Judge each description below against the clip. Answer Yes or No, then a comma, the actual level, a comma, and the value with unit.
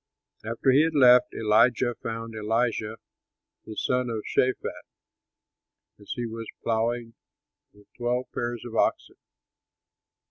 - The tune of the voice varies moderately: No, narrow, 1.7 semitones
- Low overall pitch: Yes, low, 115 Hz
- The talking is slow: Yes, slow, 115 wpm